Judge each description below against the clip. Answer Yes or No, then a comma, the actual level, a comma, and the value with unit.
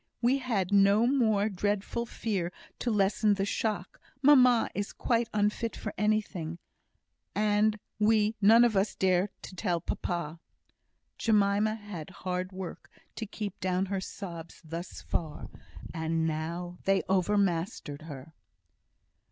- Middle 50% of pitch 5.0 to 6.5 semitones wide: No, average, 3.4 semitones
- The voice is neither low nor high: No, high, 200 Hz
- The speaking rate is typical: No, slow, 130 wpm